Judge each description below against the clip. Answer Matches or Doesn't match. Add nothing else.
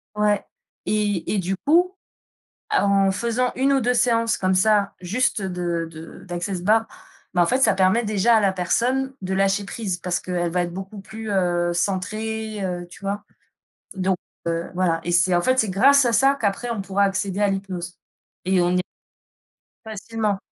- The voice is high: Matches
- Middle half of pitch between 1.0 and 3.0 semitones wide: Doesn't match